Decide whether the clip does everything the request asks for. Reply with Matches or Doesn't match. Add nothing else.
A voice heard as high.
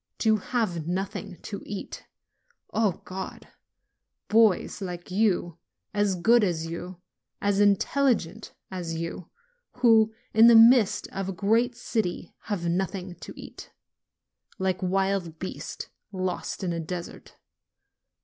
Matches